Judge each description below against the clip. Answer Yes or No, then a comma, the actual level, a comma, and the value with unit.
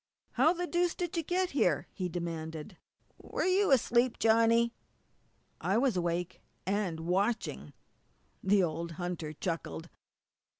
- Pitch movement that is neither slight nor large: No, wide, 7.4 semitones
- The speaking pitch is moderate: No, high, 200 Hz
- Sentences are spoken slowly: Yes, slow, 125 wpm